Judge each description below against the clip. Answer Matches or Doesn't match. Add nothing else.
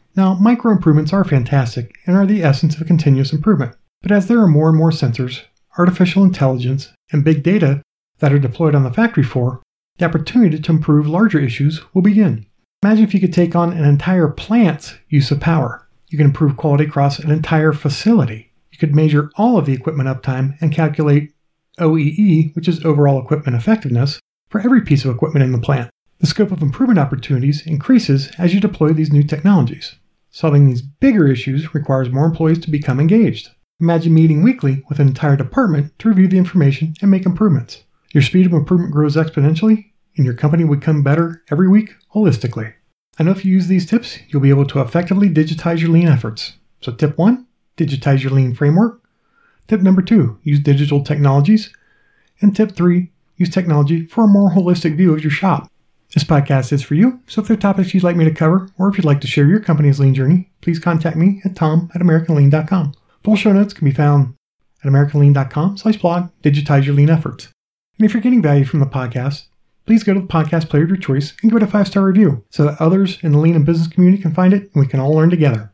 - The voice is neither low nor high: Matches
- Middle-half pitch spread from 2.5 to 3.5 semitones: Doesn't match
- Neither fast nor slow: Doesn't match